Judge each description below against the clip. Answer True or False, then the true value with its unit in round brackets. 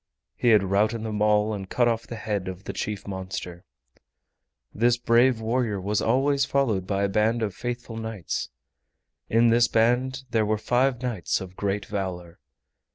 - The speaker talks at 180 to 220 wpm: False (165 wpm)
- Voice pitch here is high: False (110 Hz)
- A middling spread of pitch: True (3.2 semitones)